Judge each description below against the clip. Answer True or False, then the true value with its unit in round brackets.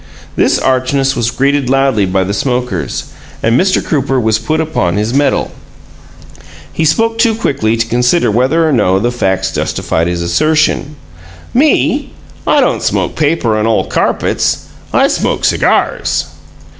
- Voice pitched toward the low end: True (125 Hz)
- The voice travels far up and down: True (5.9 semitones)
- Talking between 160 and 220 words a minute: False (145 wpm)